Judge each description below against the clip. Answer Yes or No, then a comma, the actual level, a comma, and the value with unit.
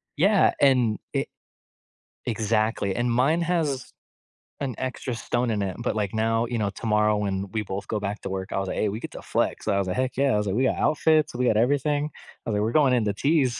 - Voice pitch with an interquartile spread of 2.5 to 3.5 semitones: No, average, 4.1 semitones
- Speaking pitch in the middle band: No, low, 115 Hz